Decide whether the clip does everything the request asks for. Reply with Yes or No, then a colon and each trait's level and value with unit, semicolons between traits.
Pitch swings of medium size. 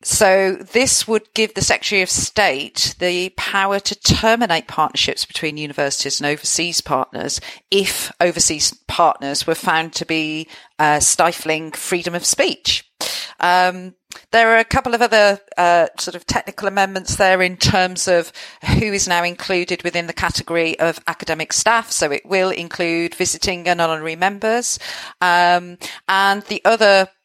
Yes: average, 3.0 semitones